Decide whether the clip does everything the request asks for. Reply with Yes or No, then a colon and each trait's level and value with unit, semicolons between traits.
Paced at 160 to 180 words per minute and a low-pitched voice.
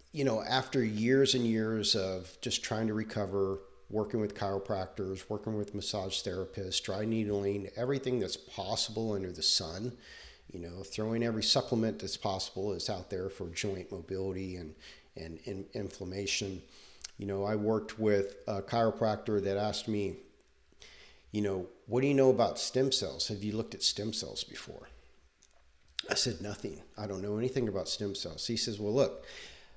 Yes: average, 165 wpm; low, 105 Hz